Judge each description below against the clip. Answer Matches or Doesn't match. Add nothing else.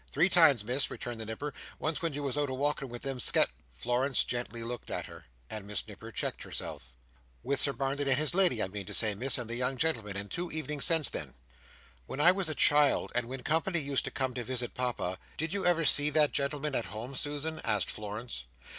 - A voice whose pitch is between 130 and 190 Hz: Matches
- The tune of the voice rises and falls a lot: Doesn't match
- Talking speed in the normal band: Doesn't match